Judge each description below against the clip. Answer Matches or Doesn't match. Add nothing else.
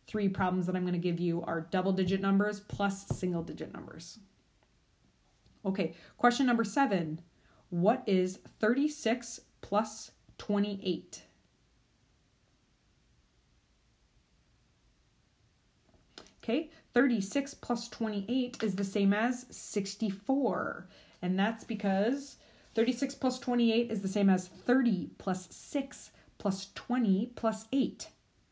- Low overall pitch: Doesn't match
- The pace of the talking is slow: Matches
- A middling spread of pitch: Matches